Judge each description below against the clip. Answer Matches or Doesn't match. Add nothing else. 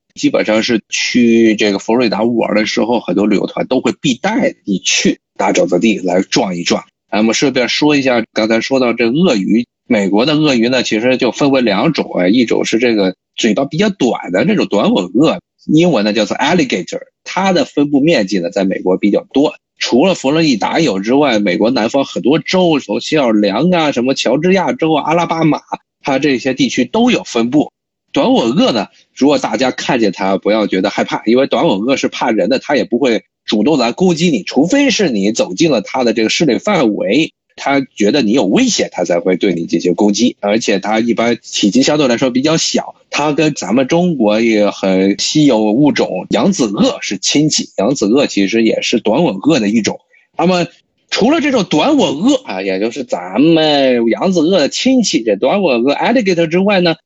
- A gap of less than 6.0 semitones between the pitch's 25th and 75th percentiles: Doesn't match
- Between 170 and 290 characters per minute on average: Doesn't match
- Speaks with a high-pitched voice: Doesn't match